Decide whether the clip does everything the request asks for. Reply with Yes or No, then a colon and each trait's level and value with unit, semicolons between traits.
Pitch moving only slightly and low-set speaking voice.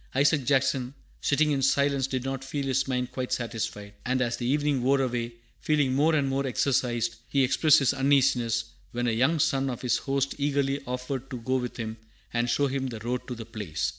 Yes: narrow, 2.2 semitones; low, 130 Hz